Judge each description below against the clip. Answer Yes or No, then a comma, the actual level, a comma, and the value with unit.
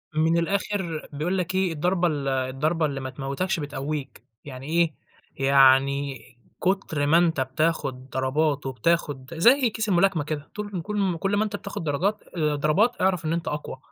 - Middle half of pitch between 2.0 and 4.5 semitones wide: No, average, 5.0 semitones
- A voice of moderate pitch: Yes, medium, 155 Hz